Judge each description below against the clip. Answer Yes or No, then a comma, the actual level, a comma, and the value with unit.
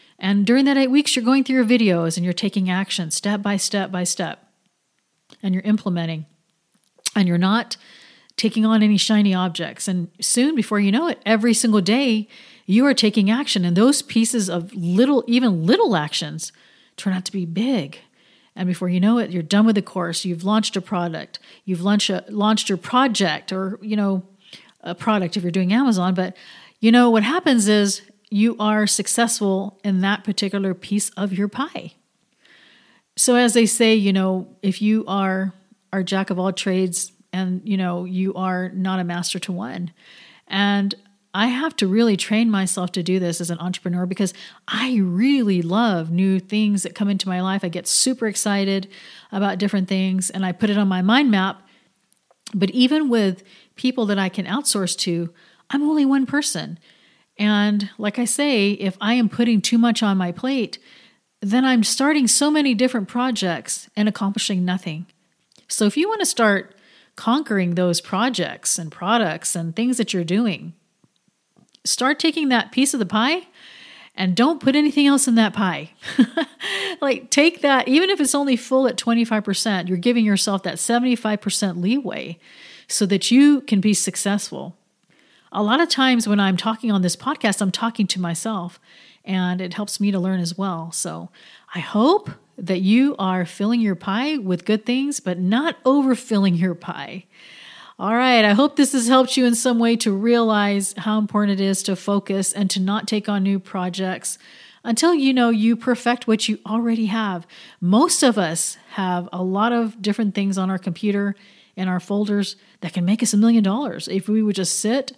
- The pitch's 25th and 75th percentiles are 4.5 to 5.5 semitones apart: No, average, 3.8 semitones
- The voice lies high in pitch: Yes, high, 205 Hz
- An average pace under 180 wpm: No, average, 185 wpm